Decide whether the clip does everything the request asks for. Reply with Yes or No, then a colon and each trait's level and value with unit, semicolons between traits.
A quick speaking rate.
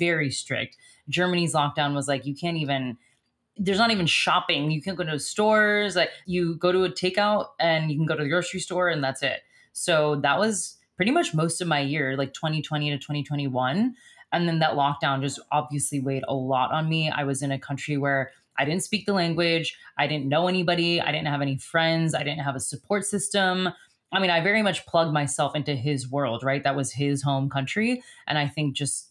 Yes: fast, 215 wpm